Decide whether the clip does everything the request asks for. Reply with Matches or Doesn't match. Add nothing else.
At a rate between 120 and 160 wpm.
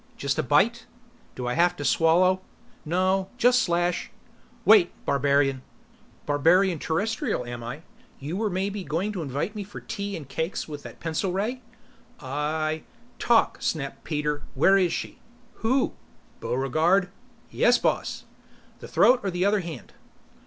Matches